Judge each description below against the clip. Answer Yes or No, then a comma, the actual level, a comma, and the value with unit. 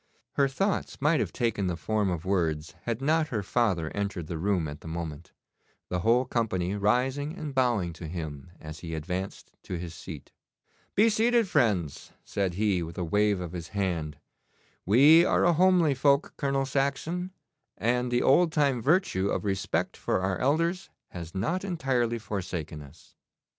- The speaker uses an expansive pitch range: Yes, wide, 8.0 semitones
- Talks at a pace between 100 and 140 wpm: No, average, 170 wpm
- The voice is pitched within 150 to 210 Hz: No, low, 105 Hz